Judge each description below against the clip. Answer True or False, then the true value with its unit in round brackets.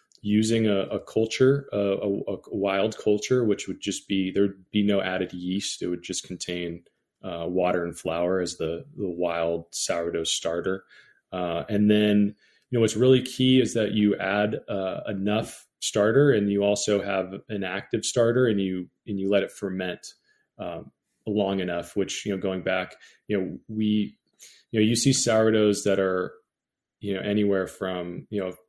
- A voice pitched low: True (100 Hz)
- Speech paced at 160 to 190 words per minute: True (180 wpm)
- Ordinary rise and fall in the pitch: False (2.3 semitones)